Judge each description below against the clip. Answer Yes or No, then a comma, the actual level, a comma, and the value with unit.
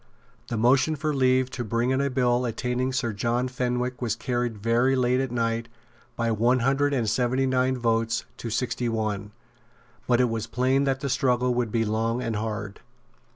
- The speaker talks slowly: No, average, 185 wpm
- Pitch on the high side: No, low, 125 Hz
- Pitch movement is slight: Yes, narrow, 2.0 semitones